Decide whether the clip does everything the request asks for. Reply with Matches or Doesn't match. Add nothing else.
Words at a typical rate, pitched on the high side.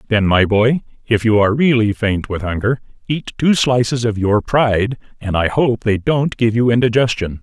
Doesn't match